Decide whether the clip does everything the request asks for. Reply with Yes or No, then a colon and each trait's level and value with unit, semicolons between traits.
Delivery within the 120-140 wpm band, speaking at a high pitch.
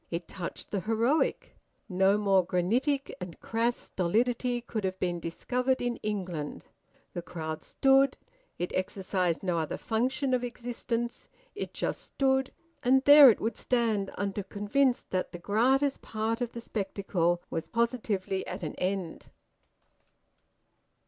Yes: slow, 135 wpm; high, 215 Hz